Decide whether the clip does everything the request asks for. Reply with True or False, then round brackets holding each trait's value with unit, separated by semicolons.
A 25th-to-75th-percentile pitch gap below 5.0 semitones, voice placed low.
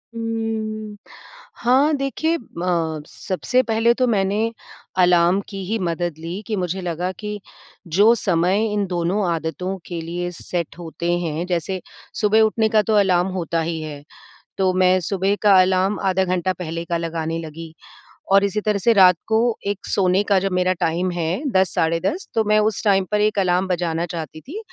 False (3.6 semitones; 185 Hz)